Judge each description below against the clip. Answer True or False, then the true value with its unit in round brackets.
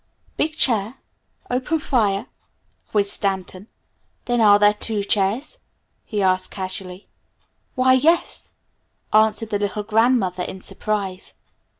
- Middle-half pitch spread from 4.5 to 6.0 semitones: False (3.7 semitones)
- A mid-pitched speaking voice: False (210 Hz)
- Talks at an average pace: False (110 wpm)